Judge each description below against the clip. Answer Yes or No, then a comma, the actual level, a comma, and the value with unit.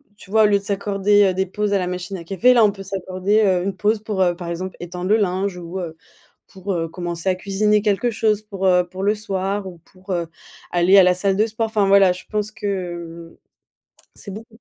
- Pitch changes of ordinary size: No, narrow, 2.3 semitones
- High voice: Yes, high, 195 Hz